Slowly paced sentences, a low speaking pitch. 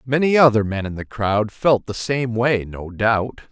No: fast, 205 wpm; low, 115 Hz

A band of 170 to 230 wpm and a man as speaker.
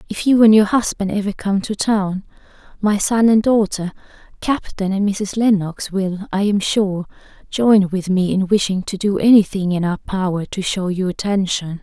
No: average, 185 wpm; female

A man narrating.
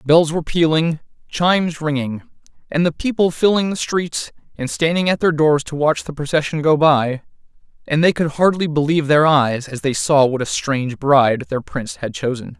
Yes: male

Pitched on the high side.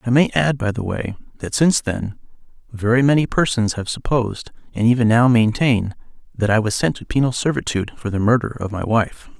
No: low, 115 Hz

